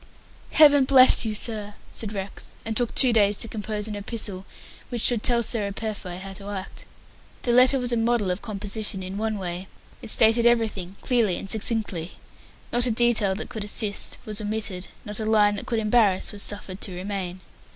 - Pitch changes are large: No, average, 2.7 semitones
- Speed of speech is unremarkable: Yes, average, 190 wpm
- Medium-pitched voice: No, high, 215 Hz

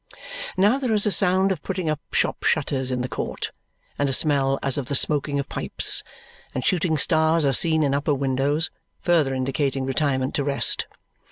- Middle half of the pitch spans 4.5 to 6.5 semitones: No, average, 3.4 semitones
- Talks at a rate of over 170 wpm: Yes, average, 185 wpm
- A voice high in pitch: No, medium, 145 Hz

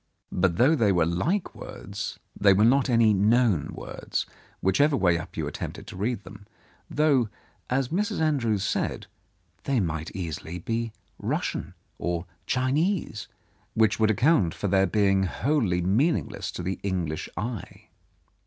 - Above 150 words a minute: No, average, 145 wpm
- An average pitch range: No, wide, 5.7 semitones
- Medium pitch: No, low, 105 Hz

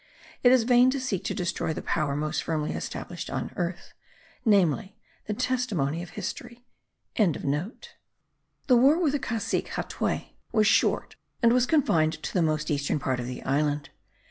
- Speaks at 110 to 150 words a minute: No, average, 160 wpm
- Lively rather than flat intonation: Yes, wide, 8.2 semitones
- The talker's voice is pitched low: No, medium, 185 Hz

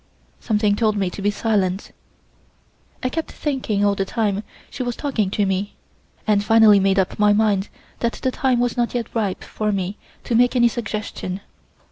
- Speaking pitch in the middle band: No, high, 210 Hz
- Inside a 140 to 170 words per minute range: No, average, 180 wpm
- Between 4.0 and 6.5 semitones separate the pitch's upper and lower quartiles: No, average, 3.0 semitones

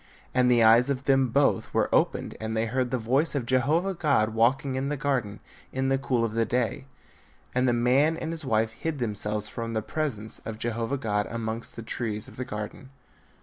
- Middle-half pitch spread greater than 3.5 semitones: No, average, 3.2 semitones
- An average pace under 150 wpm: No, fast, 205 wpm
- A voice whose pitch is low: Yes, low, 125 Hz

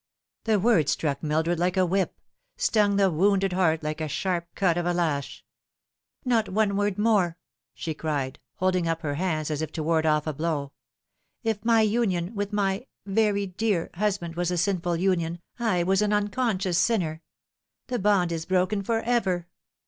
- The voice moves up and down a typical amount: Yes, average, 3.8 semitones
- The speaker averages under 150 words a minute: No, average, 180 wpm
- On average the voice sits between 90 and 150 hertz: No, medium, 185 Hz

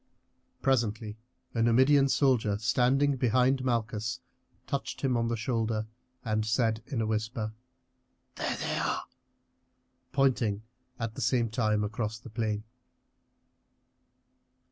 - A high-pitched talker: No, low, 115 Hz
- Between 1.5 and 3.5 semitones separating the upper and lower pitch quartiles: Yes, average, 2.8 semitones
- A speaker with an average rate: No, slow, 115 wpm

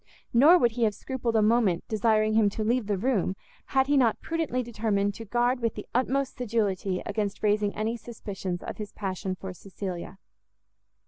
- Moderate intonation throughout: Yes, average, 3.2 semitones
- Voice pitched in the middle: No, high, 215 Hz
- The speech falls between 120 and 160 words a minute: No, average, 180 wpm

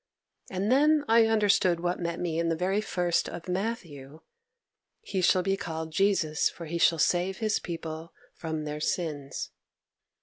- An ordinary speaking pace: Yes, average, 160 wpm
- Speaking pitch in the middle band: Yes, medium, 175 Hz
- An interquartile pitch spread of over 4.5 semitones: No, average, 3.4 semitones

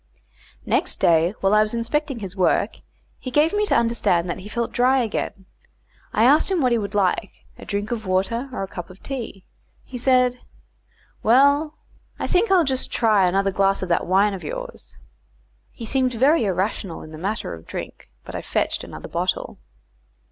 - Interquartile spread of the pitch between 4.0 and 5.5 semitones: Yes, average, 5.2 semitones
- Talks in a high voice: Yes, high, 225 Hz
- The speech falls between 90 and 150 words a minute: No, average, 185 wpm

